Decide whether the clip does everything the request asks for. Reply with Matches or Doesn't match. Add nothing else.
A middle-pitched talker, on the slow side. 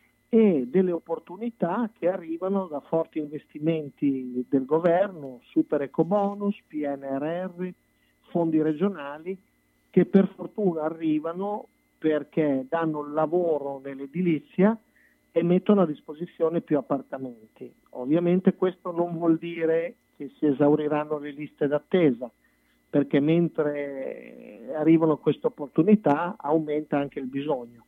Matches